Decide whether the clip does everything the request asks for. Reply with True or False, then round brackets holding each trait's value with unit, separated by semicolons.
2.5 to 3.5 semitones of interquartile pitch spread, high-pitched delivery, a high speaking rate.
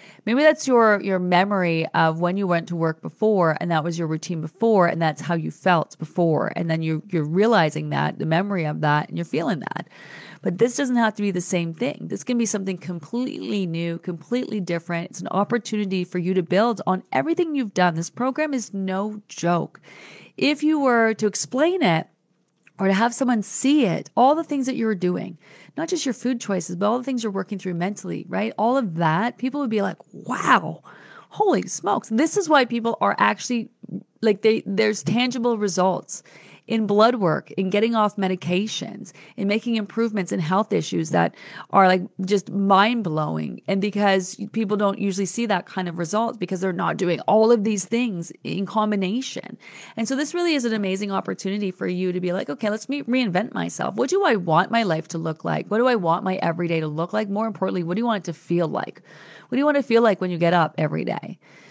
False (4.6 semitones; 200 Hz; 220 wpm)